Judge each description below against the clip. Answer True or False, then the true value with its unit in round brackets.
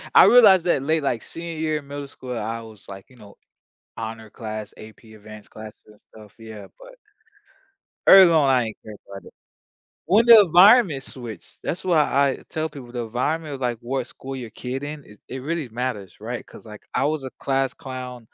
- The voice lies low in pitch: True (130 Hz)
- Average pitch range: False (5.8 semitones)